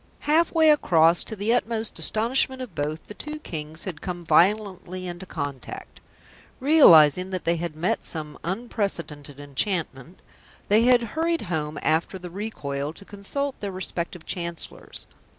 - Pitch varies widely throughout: Yes, wide, 5.8 semitones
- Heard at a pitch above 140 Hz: Yes, medium, 185 Hz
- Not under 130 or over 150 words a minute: Yes, average, 145 wpm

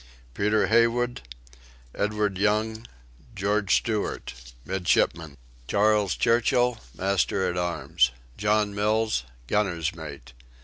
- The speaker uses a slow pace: Yes, slow, 90 wpm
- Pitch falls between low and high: No, low, 105 Hz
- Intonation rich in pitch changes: No, average, 3.6 semitones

